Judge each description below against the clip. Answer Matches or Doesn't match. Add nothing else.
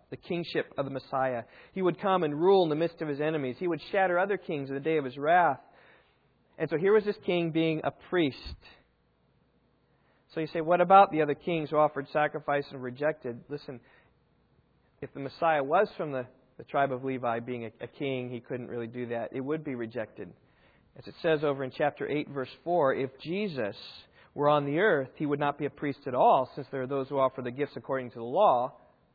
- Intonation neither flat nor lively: Matches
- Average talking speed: Doesn't match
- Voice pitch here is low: Doesn't match